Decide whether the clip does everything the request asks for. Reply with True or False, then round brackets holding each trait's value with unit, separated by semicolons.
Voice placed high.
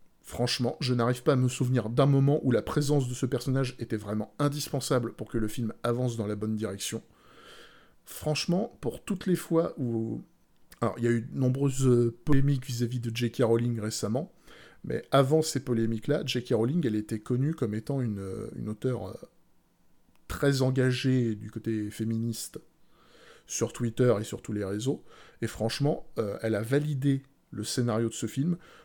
False (120 Hz)